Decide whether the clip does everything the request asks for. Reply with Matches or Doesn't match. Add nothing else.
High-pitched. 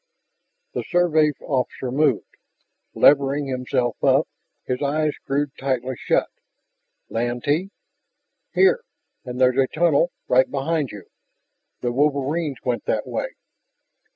Doesn't match